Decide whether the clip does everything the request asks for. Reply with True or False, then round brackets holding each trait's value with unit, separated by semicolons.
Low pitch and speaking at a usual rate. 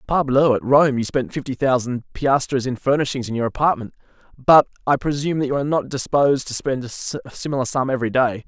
True (130 Hz; 190 wpm)